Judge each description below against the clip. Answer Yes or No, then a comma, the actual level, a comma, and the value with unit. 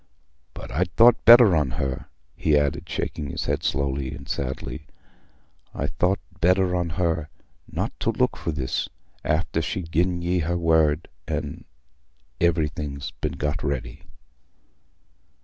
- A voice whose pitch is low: Yes, very low, 80 Hz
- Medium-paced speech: No, slow, 130 wpm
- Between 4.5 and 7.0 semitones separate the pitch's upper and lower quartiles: No, average, 3.4 semitones